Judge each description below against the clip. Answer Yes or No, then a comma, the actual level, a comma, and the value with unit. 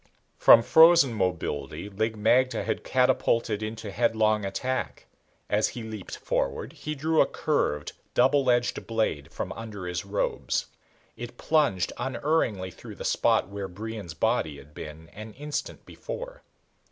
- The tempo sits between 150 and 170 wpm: No, average, 140 wpm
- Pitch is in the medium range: No, low, 110 Hz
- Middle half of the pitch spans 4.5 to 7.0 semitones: Yes, average, 4.9 semitones